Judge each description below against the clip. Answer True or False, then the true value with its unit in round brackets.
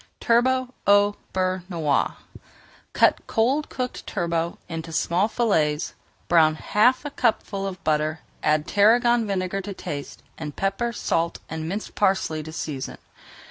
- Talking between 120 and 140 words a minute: True (135 wpm)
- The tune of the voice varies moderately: False (5.7 semitones)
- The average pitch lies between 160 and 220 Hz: True (190 Hz)